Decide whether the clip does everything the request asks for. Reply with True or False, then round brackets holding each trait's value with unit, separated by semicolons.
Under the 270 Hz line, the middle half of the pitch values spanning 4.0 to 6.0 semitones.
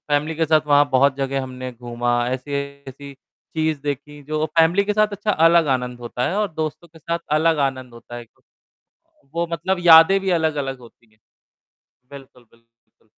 True (140 Hz; 4.4 semitones)